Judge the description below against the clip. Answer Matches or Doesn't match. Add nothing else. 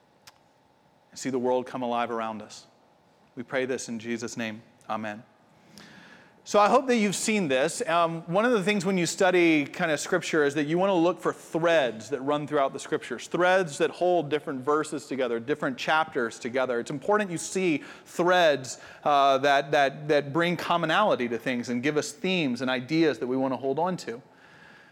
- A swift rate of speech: Doesn't match